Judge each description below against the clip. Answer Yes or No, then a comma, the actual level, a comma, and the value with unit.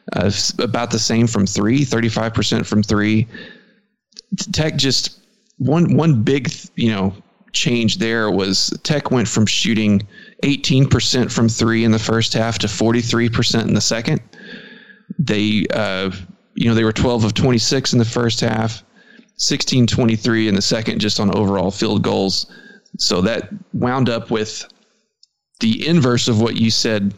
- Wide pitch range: Yes, wide, 6.3 semitones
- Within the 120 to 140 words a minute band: No, average, 150 wpm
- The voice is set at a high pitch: No, low, 115 Hz